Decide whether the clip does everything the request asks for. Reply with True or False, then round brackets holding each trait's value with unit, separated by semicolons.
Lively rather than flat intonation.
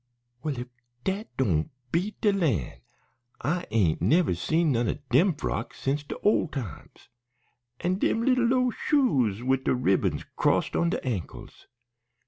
True (8.3 semitones)